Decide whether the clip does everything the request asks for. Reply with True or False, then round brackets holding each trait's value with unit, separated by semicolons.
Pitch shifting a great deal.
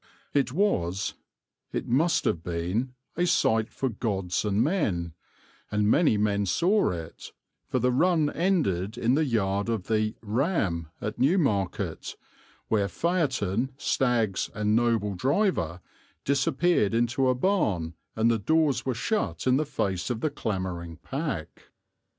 True (6.4 semitones)